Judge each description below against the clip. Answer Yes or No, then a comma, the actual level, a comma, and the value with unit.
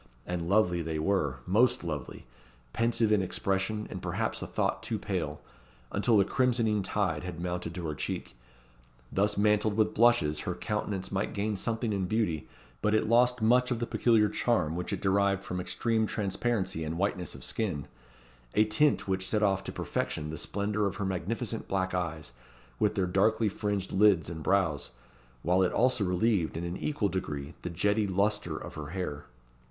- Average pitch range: Yes, average, 3.4 semitones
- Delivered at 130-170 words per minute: No, average, 180 wpm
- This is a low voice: Yes, low, 100 Hz